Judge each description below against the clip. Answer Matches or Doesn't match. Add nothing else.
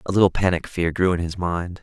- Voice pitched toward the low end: Matches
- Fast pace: Matches